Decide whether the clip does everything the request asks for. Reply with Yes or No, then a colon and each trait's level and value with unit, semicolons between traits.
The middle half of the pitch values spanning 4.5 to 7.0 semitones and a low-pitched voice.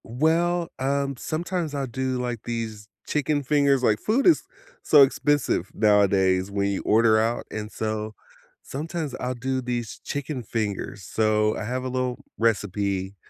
Yes: average, 4.8 semitones; low, 125 Hz